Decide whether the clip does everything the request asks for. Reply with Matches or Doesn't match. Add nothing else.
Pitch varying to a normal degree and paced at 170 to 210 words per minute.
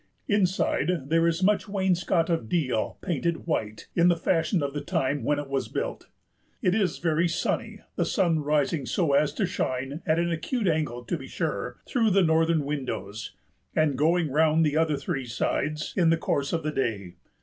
Matches